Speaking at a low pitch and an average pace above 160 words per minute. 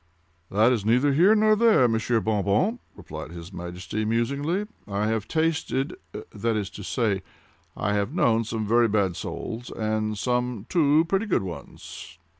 No: low, 115 Hz; average, 150 wpm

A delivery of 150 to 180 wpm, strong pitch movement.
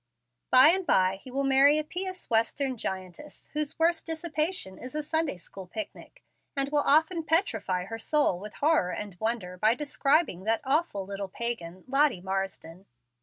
Yes: average, 165 wpm; wide, 8.0 semitones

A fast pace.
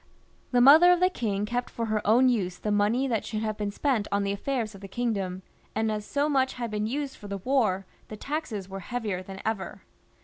Yes: fast, 230 wpm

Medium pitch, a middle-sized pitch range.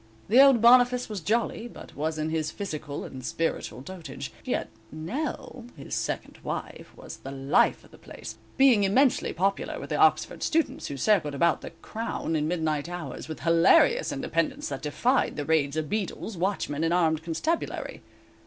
No: medium, 170 Hz; wide, 7.2 semitones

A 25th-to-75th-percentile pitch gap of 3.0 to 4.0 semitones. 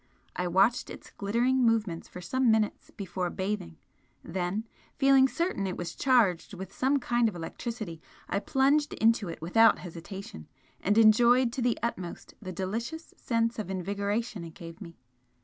No: average, 4.8 semitones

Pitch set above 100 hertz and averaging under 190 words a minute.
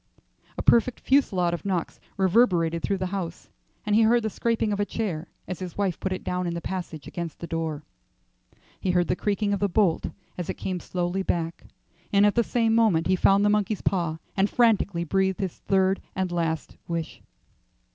No: high, 190 Hz; average, 195 wpm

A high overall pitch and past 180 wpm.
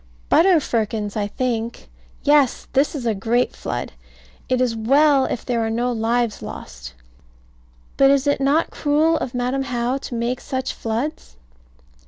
No: high, 245 Hz; average, 155 wpm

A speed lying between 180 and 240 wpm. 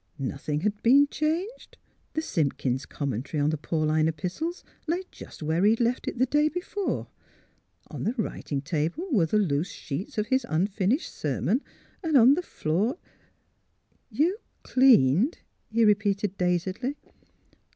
No: average, 160 wpm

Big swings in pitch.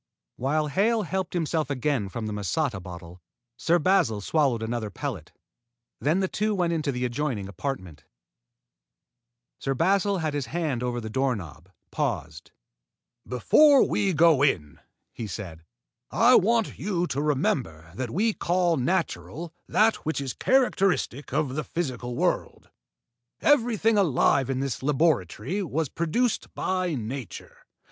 Yes: wide, 7.2 semitones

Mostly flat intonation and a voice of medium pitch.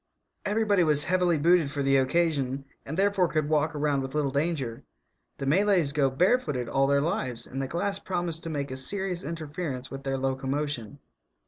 No: average, 4.3 semitones; medium, 150 Hz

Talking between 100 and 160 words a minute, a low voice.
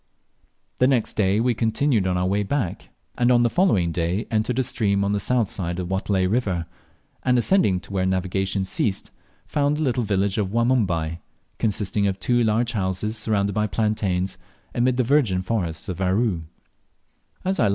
No: average, 170 wpm; low, 105 Hz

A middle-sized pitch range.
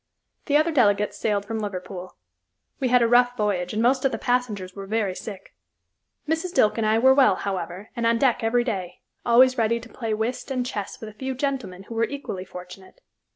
Yes: average, 3.8 semitones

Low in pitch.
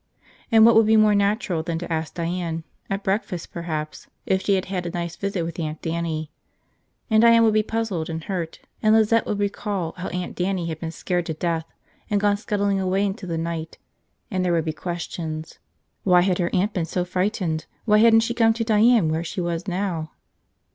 No: medium, 180 Hz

